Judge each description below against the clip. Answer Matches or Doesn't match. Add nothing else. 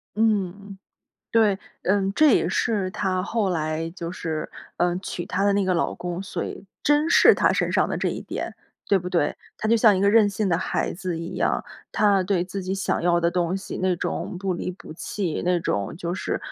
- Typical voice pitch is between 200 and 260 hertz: Doesn't match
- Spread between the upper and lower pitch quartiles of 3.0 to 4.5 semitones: Doesn't match